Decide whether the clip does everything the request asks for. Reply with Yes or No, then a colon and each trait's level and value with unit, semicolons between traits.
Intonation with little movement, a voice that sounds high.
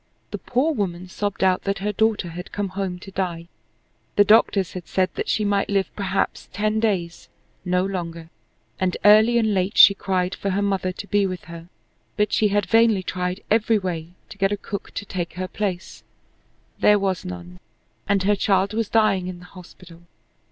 Yes: narrow, 2.3 semitones; high, 195 Hz